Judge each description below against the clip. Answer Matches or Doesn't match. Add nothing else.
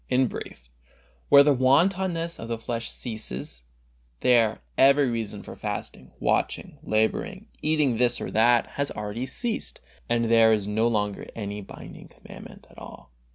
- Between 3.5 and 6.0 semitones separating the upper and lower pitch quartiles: Matches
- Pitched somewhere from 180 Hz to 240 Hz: Doesn't match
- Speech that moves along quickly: Doesn't match